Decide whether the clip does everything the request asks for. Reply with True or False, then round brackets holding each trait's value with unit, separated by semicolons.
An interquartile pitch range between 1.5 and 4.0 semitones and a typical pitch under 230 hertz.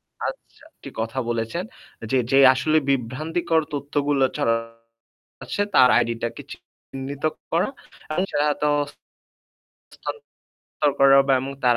False (4.6 semitones; 135 Hz)